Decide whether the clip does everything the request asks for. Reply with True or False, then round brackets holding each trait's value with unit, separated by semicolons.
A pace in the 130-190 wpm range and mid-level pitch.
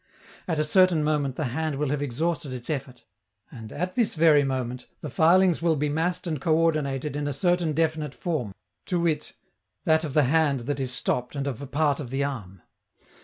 False (200 wpm; 150 Hz)